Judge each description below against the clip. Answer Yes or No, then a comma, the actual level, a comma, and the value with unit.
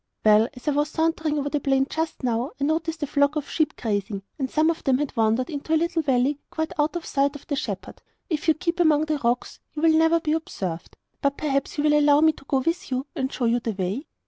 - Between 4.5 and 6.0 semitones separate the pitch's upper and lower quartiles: No, average, 3.6 semitones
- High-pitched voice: Yes, very high, 290 Hz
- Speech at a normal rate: No, fast, 250 wpm